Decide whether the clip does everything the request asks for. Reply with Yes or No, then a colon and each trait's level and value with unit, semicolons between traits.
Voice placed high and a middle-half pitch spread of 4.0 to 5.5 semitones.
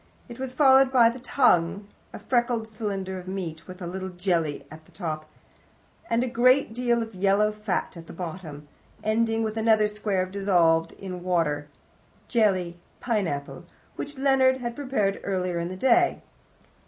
Yes: high, 200 Hz; average, 5.0 semitones